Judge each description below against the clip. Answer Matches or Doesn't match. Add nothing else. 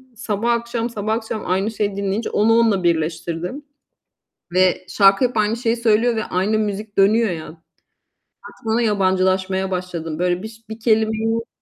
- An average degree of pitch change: Matches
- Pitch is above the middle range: Matches